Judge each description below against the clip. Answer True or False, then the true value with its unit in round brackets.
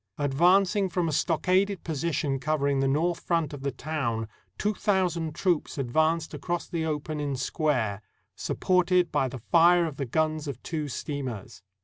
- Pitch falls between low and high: True (155 Hz)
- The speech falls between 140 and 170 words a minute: True (160 wpm)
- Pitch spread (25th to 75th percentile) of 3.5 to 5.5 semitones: True (3.9 semitones)